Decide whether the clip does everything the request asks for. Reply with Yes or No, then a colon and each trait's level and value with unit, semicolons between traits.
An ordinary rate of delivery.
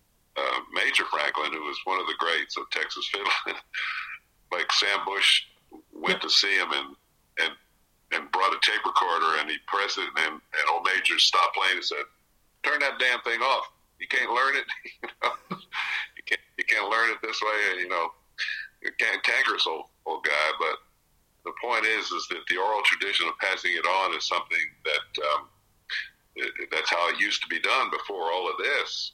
Yes: average, 195 wpm